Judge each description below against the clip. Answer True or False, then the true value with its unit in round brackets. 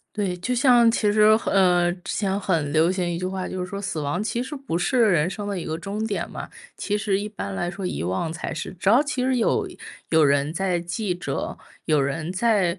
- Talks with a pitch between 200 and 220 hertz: False (190 Hz)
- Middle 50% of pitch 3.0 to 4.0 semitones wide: True (3.7 semitones)